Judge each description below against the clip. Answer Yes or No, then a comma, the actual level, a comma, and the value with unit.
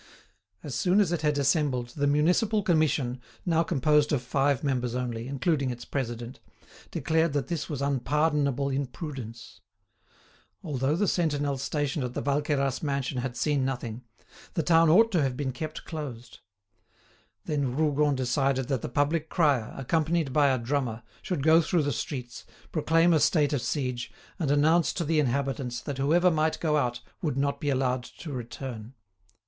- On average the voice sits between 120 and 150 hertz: Yes, medium, 140 Hz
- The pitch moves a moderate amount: Yes, average, 3.4 semitones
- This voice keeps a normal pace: Yes, average, 165 wpm